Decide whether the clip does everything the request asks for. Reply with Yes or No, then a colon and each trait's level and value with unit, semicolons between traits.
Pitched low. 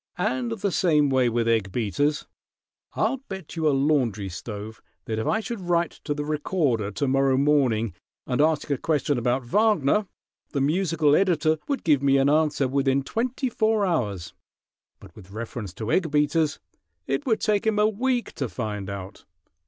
No: medium, 145 Hz